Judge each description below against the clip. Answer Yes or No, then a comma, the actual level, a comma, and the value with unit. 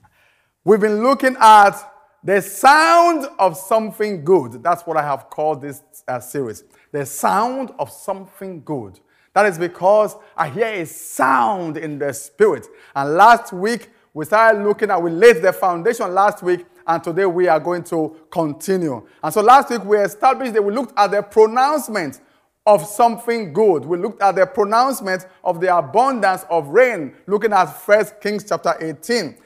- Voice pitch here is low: No, high, 200 Hz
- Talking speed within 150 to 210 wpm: Yes, average, 170 wpm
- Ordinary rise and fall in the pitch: Yes, average, 4.7 semitones